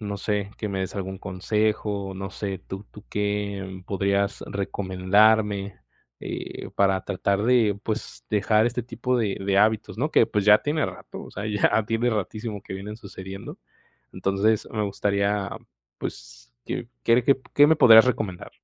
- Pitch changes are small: Yes, narrow, 2.0 semitones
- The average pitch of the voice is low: Yes, low, 105 Hz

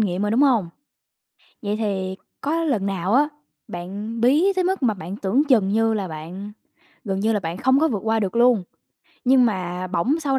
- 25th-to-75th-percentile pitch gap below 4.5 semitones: No, average, 5.2 semitones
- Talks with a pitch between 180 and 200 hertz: No, high, 215 Hz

